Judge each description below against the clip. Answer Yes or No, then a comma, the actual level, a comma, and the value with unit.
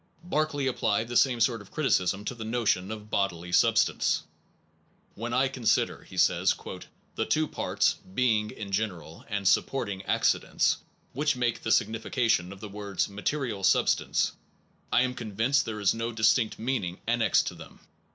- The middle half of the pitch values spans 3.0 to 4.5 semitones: Yes, average, 3.7 semitones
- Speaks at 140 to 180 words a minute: Yes, average, 160 wpm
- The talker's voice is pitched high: No, low, 110 Hz